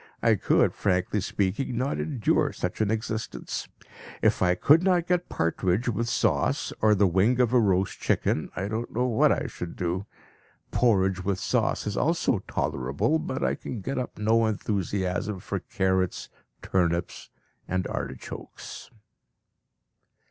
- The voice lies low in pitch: Yes, low, 105 Hz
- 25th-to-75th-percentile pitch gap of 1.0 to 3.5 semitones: No, average, 4.5 semitones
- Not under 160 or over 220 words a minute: No, average, 145 wpm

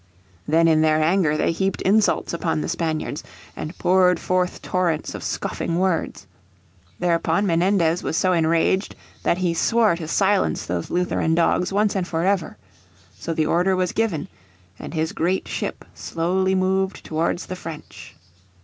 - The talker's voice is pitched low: No, medium, 175 Hz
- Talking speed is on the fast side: No, average, 155 wpm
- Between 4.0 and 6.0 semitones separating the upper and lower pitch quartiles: No, narrow, 2.6 semitones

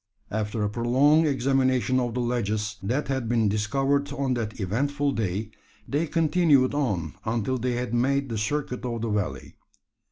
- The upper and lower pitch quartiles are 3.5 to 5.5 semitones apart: Yes, average, 4.2 semitones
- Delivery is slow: No, average, 160 wpm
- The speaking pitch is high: No, low, 125 Hz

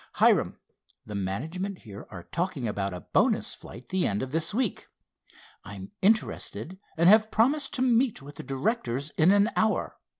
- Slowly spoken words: No, average, 165 wpm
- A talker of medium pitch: Yes, medium, 170 Hz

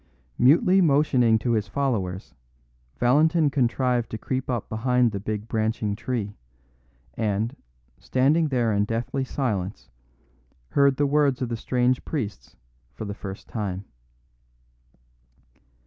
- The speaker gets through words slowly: Yes, slow, 120 wpm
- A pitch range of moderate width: Yes, average, 4.1 semitones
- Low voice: Yes, low, 120 Hz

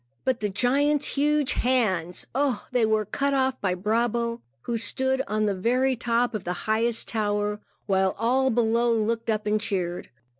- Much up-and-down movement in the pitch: No, average, 3.5 semitones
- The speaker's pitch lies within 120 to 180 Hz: No, high, 230 Hz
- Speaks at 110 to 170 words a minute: Yes, average, 165 wpm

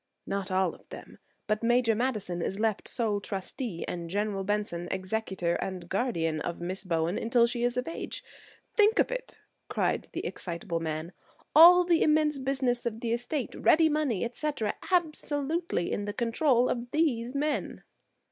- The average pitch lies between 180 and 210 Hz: No, high, 230 Hz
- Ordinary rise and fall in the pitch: No, wide, 6.6 semitones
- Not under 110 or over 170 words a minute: Yes, average, 160 wpm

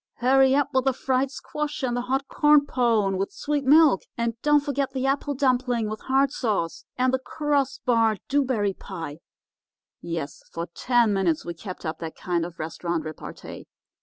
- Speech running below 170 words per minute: No, average, 180 wpm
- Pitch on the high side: Yes, very high, 250 Hz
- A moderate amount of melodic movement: No, wide, 6.0 semitones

